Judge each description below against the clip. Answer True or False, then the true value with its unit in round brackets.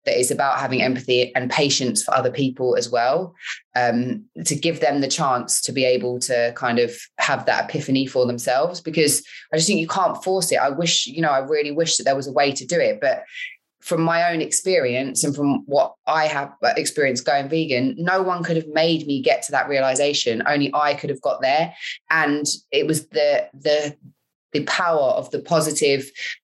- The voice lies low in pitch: False (145 Hz)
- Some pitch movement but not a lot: True (3.7 semitones)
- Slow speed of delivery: False (205 wpm)